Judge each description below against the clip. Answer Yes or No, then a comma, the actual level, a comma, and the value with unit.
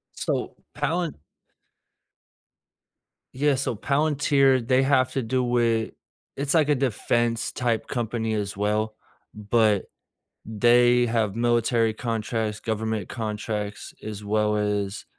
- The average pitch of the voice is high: No, low, 115 Hz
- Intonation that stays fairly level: No, average, 3.1 semitones